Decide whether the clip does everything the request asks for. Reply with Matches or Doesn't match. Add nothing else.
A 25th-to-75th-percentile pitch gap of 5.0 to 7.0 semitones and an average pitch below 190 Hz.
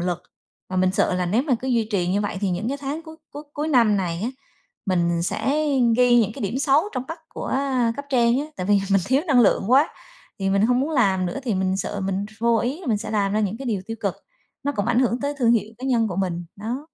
Doesn't match